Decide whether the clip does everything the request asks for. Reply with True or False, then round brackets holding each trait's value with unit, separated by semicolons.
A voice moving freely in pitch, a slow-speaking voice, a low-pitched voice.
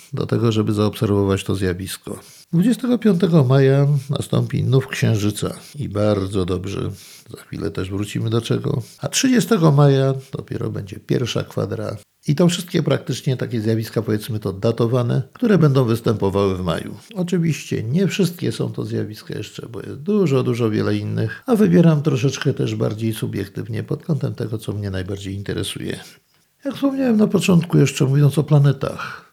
False (6.4 semitones; 155 wpm; 130 Hz)